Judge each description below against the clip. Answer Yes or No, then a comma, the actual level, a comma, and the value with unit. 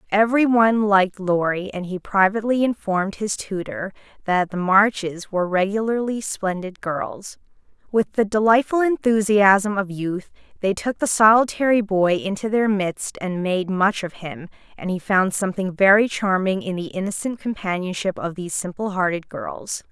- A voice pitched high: Yes, high, 200 Hz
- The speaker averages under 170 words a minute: Yes, average, 155 wpm